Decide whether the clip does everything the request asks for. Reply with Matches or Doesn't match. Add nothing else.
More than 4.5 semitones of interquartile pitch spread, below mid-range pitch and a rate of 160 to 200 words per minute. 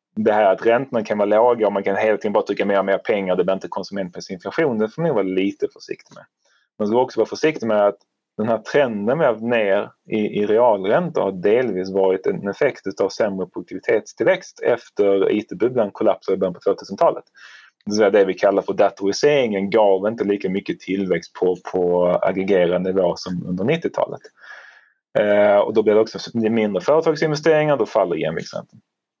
Matches